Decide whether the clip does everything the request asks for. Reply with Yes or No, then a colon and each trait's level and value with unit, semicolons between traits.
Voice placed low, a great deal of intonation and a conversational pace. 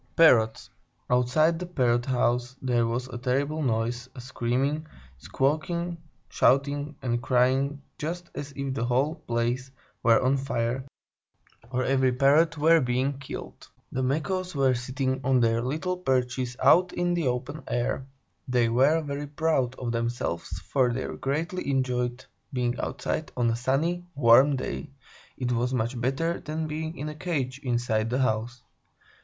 No: low, 130 Hz; average, 3.4 semitones; average, 150 wpm